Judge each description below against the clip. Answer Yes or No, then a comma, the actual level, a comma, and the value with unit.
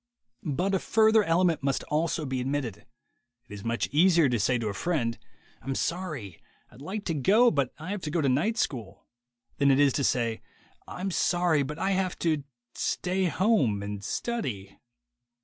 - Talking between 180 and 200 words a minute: Yes, average, 185 wpm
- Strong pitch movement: Yes, wide, 6.9 semitones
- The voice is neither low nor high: Yes, medium, 145 Hz